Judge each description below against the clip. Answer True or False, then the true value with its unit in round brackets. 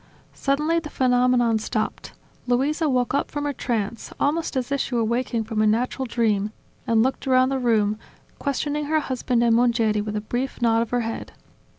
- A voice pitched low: False (245 Hz)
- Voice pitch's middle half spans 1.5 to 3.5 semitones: True (3.1 semitones)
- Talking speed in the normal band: True (190 wpm)